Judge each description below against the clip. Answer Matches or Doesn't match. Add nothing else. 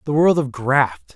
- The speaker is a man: Matches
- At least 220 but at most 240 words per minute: Doesn't match